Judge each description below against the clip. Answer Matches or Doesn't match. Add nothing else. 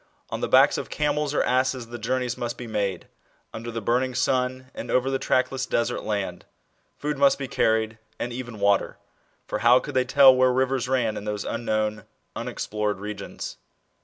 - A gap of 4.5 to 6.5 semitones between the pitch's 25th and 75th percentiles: Doesn't match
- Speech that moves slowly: Doesn't match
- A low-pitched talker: Matches